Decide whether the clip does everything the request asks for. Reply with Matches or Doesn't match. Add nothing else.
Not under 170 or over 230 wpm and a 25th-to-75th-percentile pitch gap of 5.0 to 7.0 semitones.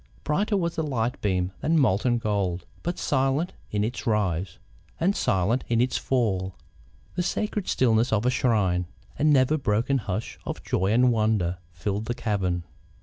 Doesn't match